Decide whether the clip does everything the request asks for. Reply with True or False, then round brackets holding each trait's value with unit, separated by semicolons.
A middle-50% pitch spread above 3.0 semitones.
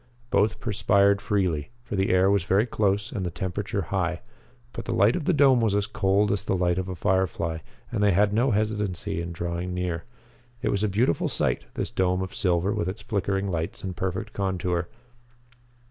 False (2.4 semitones)